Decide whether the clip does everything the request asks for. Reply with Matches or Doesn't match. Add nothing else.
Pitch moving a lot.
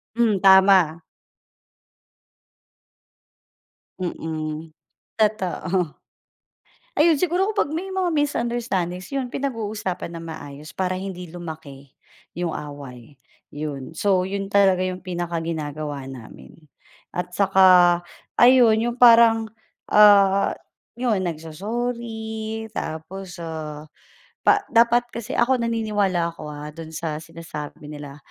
Matches